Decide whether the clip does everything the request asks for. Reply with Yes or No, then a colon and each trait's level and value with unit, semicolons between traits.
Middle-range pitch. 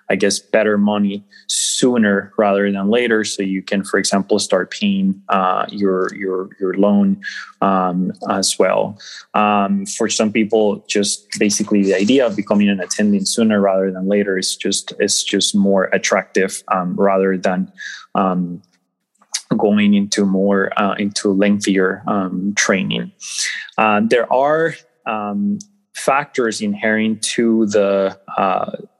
No: low, 100 Hz